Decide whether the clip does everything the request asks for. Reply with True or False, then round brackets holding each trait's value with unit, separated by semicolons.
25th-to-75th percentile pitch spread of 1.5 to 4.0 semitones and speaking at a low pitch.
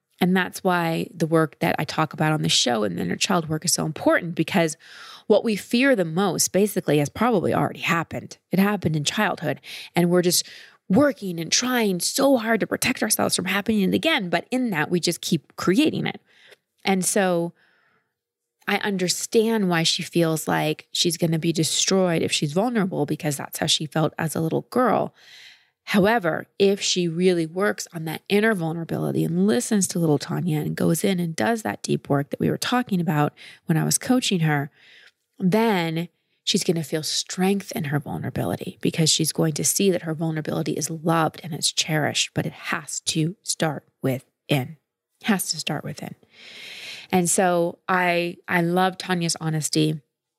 False (3.7 semitones; 175 Hz)